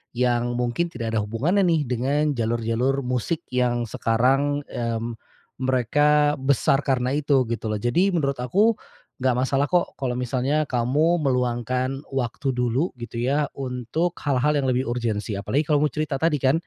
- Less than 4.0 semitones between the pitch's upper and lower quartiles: Yes, average, 3.3 semitones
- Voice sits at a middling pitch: No, low, 130 Hz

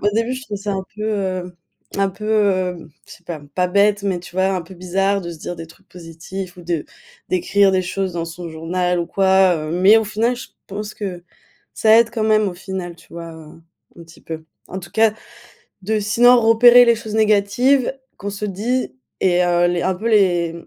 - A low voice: No, high, 190 Hz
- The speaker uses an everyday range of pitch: Yes, average, 3.3 semitones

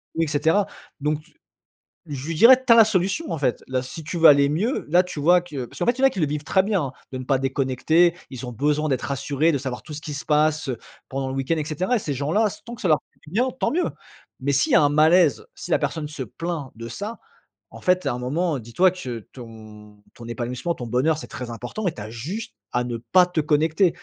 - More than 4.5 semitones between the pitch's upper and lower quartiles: Yes, average, 5.2 semitones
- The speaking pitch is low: No, medium, 150 Hz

